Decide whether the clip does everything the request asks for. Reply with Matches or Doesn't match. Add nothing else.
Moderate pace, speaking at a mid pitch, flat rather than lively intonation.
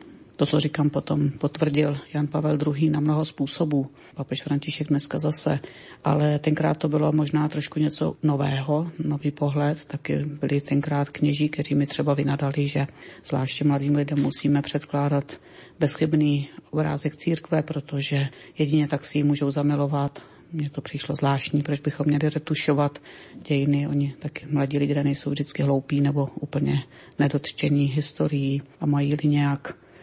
Matches